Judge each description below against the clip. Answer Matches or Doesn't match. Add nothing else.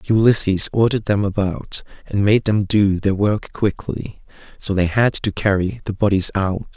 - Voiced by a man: Matches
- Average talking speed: Matches